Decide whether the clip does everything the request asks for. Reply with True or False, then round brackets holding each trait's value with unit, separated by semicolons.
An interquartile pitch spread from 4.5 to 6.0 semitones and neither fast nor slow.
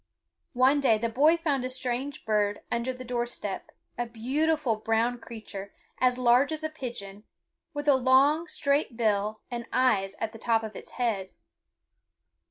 False (3.5 semitones; 165 wpm)